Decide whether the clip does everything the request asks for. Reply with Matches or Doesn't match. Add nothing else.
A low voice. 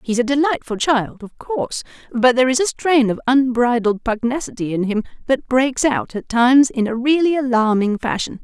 Doesn't match